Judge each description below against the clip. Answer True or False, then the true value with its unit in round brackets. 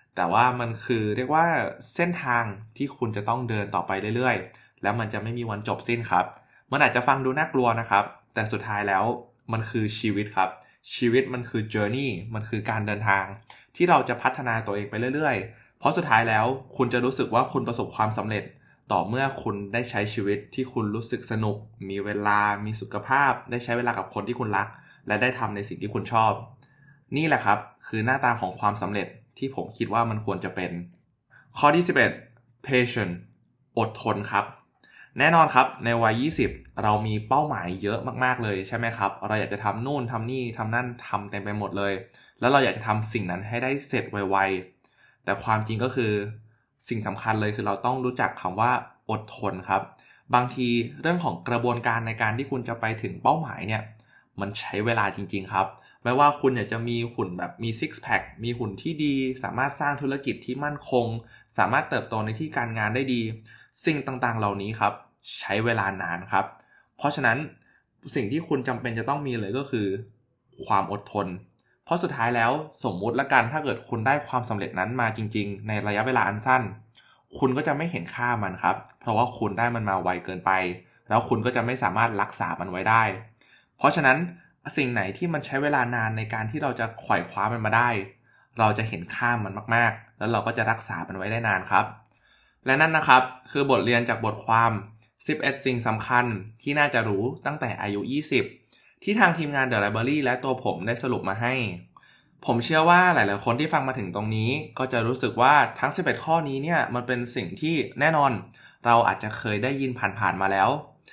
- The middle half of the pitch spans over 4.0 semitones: False (3.7 semitones)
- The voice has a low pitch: True (115 Hz)